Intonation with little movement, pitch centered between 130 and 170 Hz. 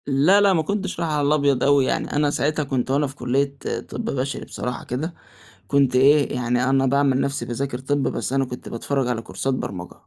Yes: narrow, 2.1 semitones; medium, 140 Hz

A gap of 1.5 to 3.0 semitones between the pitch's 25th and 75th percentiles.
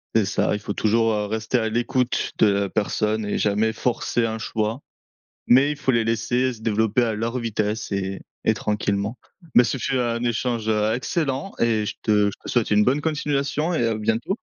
Yes: narrow, 2.6 semitones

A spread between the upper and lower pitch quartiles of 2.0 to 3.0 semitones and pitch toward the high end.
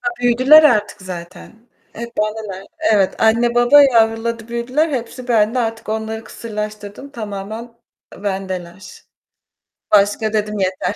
Yes: narrow, 2.5 semitones; high, 220 Hz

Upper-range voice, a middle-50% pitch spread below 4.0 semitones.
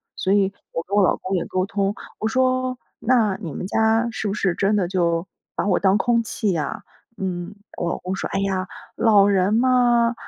Yes: high, 200 Hz; average, 3.3 semitones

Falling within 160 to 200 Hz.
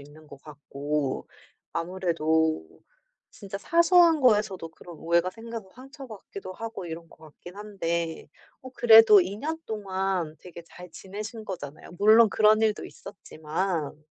Yes: high, 190 Hz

